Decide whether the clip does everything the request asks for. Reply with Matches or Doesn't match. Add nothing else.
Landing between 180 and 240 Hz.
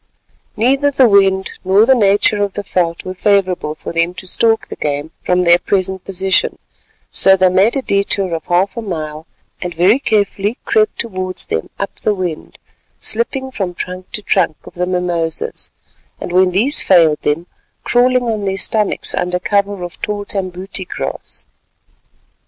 Matches